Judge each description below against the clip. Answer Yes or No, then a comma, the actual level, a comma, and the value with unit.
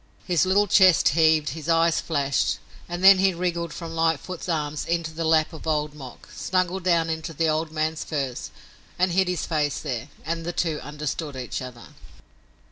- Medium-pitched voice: Yes, medium, 160 Hz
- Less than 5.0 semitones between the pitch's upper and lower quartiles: Yes, narrow, 2.4 semitones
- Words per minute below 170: No, average, 180 wpm